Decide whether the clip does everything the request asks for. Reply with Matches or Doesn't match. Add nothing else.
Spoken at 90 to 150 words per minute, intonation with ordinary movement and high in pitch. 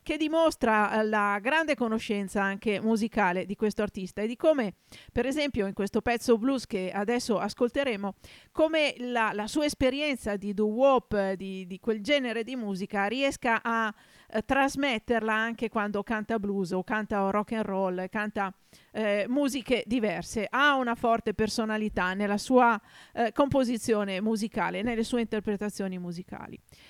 Matches